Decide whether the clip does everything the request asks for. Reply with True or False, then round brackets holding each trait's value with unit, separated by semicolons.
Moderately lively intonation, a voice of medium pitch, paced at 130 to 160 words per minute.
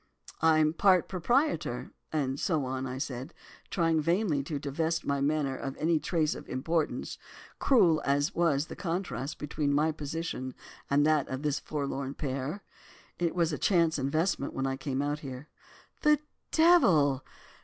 True (3.3 semitones; 150 Hz; 155 wpm)